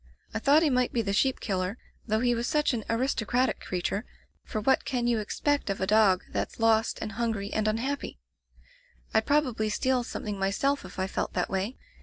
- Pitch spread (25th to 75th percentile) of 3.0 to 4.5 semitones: Yes, average, 3.8 semitones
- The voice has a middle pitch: No, high, 225 Hz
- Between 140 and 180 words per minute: No, fast, 205 wpm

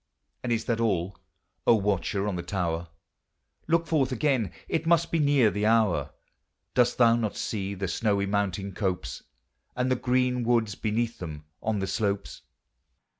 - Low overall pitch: Yes, low, 110 Hz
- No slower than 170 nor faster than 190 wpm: No, average, 160 wpm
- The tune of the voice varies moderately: Yes, average, 4.0 semitones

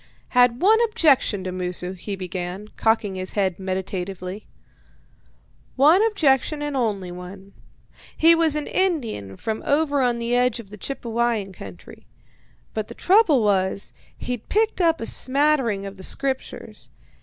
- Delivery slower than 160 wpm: Yes, average, 145 wpm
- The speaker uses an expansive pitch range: Yes, wide, 7.1 semitones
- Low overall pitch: No, high, 230 Hz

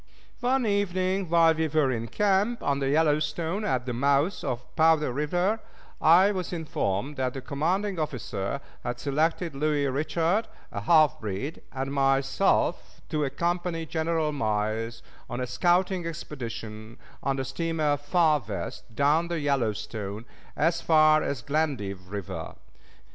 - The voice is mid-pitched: Yes, medium, 150 Hz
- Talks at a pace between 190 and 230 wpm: No, slow, 135 wpm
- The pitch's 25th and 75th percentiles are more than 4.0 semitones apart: Yes, average, 4.6 semitones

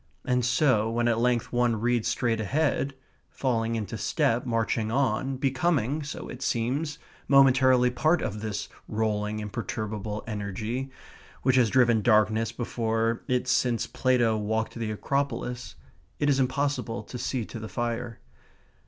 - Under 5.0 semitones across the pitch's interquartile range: Yes, average, 2.8 semitones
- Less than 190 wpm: Yes, average, 140 wpm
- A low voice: Yes, low, 120 Hz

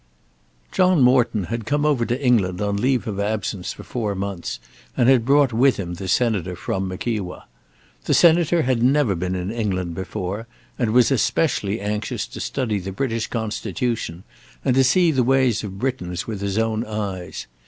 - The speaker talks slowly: No, average, 175 wpm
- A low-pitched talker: Yes, low, 110 Hz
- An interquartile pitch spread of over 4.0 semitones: Yes, average, 4.7 semitones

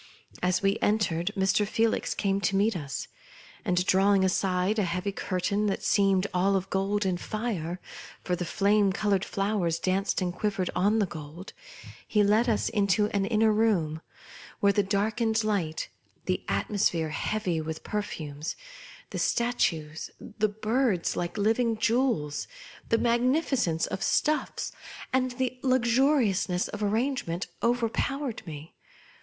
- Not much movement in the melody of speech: No, average, 3.5 semitones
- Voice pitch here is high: Yes, high, 200 Hz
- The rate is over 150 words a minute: No, average, 145 wpm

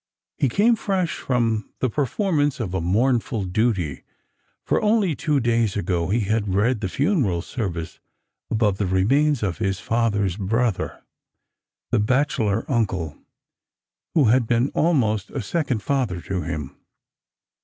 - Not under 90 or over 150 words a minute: Yes, average, 140 wpm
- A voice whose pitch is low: Yes, low, 115 Hz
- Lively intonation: Yes, wide, 5.8 semitones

